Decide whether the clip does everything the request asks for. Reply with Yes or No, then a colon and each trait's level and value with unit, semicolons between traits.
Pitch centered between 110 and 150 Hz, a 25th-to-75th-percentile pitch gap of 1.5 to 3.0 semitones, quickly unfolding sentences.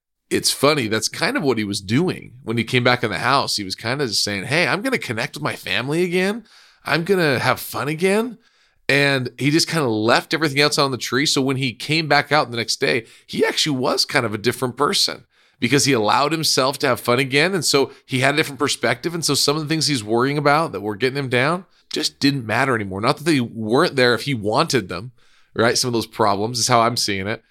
No: low, 135 Hz; average, 4.0 semitones; fast, 250 wpm